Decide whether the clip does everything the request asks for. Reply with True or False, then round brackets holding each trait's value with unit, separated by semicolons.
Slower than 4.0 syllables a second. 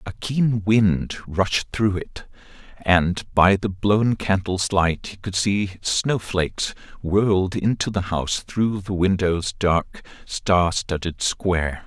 True (3.4 syllables/s)